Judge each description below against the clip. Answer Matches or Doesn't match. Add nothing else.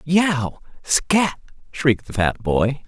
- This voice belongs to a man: Matches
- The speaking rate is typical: Doesn't match